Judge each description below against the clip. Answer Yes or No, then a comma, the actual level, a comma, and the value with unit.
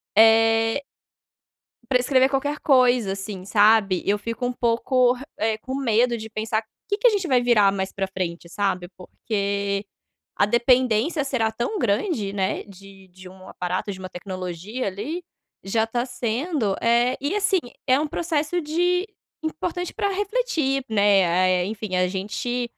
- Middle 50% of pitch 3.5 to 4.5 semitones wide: No, average, 5.3 semitones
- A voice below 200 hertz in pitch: No, high, 225 Hz